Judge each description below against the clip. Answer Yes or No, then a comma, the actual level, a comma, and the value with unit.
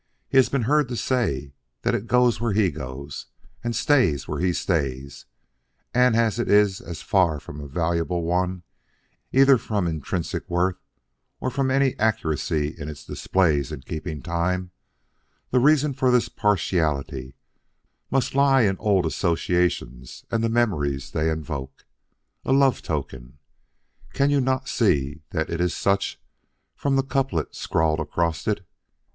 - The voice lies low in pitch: Yes, very low, 90 Hz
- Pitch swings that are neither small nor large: No, wide, 7.9 semitones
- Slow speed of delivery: No, average, 145 wpm